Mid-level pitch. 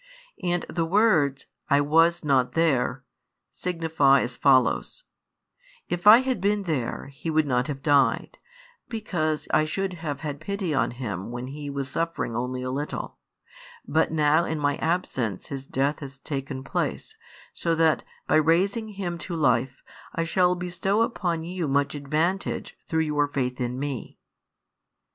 Yes: medium, 155 Hz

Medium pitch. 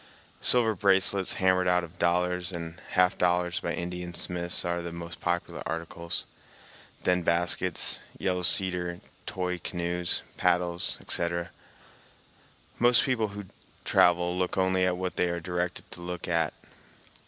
No: very low, 90 Hz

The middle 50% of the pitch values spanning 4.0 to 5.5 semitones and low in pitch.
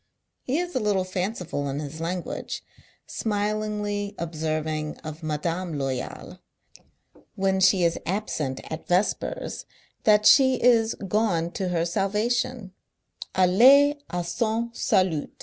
No: average, 4.7 semitones; high, 190 Hz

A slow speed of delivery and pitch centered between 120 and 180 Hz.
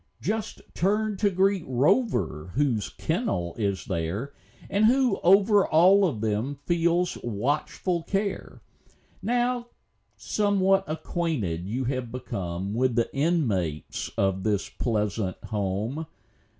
Yes: slow, 110 wpm; medium, 140 Hz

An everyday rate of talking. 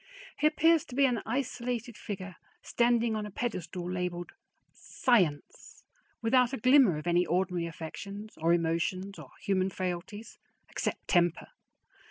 Yes: average, 165 wpm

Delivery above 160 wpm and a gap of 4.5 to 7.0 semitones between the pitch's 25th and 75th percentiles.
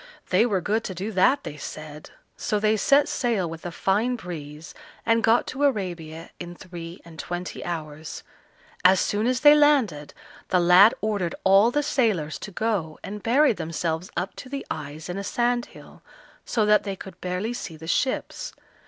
Yes: average, 180 wpm; wide, 5.4 semitones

